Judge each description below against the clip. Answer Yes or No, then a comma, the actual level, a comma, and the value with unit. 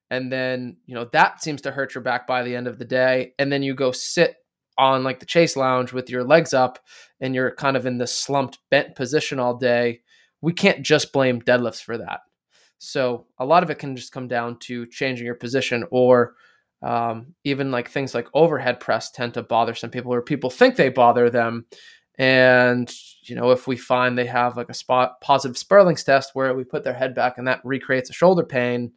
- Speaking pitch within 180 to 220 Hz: No, low, 130 Hz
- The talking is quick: Yes, fast, 220 wpm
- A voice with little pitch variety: Yes, narrow, 1.9 semitones